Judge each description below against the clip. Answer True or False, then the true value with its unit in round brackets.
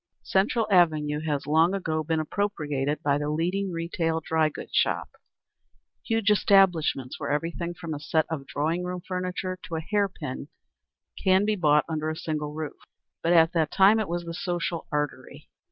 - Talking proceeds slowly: False (170 wpm)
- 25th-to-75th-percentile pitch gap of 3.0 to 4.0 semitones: True (3.3 semitones)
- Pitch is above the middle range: False (165 Hz)